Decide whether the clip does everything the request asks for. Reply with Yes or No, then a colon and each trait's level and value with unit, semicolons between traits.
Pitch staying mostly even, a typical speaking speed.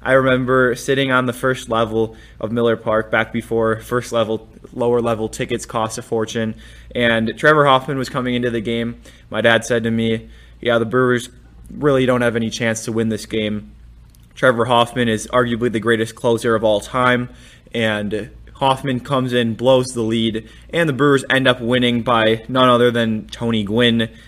Yes: narrow, 2.0 semitones; average, 185 wpm